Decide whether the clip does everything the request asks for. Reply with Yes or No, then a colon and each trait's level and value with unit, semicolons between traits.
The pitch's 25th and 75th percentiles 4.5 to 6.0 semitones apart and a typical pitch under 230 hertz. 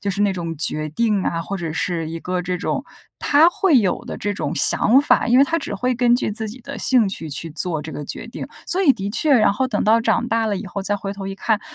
Yes: average, 5.2 semitones; high, 205 Hz